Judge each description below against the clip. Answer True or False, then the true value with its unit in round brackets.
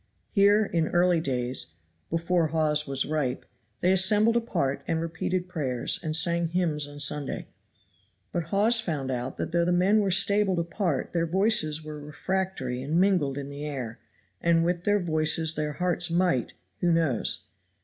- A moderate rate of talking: True (160 wpm)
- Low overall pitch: False (165 Hz)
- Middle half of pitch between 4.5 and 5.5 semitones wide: False (3.6 semitones)